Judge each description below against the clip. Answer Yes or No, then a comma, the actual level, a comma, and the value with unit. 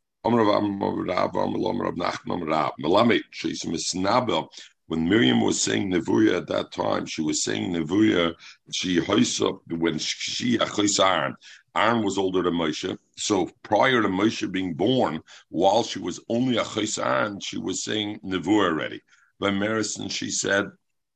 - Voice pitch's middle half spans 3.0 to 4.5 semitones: Yes, average, 4.1 semitones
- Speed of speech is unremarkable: No, slow, 115 wpm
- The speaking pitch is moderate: No, low, 100 Hz